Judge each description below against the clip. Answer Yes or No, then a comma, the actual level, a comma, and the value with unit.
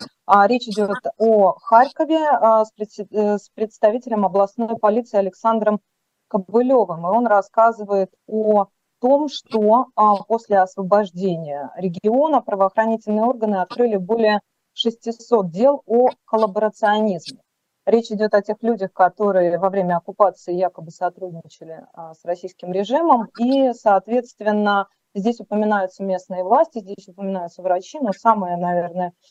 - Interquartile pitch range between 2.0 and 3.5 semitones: Yes, average, 3.1 semitones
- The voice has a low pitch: No, high, 210 Hz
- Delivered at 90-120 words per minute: Yes, slow, 110 wpm